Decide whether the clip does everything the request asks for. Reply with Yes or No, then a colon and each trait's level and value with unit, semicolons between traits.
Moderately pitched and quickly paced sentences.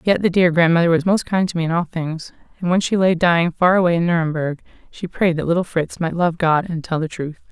Yes: medium, 170 Hz; fast, 265 wpm